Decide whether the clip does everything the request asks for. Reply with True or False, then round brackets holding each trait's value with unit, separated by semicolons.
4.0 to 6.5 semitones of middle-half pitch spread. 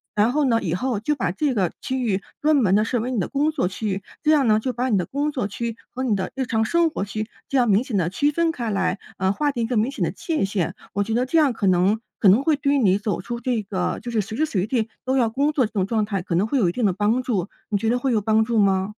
True (4.7 semitones)